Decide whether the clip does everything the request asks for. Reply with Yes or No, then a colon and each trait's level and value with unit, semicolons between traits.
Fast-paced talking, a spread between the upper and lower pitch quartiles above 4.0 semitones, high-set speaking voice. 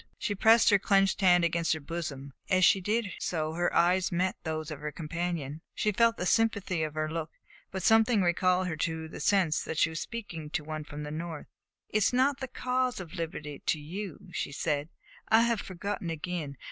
No: fast, 210 wpm; average, 4.4 semitones; medium, 175 Hz